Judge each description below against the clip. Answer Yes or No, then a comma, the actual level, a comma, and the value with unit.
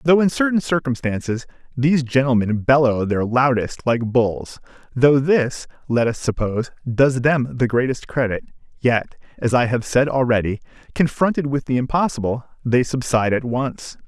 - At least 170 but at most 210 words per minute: No, average, 150 wpm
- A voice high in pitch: No, low, 130 Hz